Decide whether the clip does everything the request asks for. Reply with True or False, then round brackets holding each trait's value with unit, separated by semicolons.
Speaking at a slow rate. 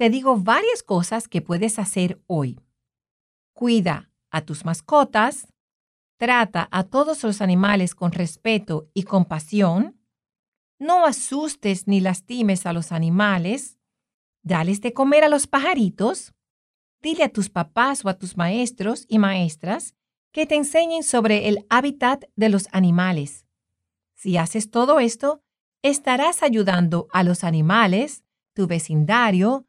True (130 wpm)